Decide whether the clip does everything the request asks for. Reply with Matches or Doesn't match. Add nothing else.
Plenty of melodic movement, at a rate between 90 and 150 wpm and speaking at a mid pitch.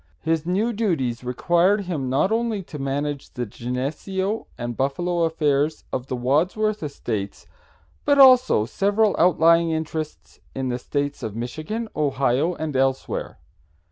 Matches